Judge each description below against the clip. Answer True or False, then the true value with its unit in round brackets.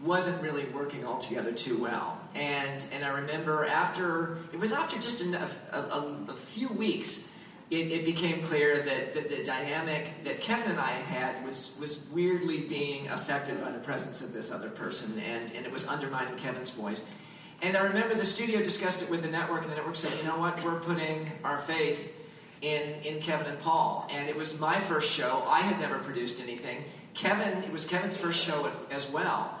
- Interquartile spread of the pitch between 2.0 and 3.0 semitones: False (3.6 semitones)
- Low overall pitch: False (155 Hz)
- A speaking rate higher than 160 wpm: True (200 wpm)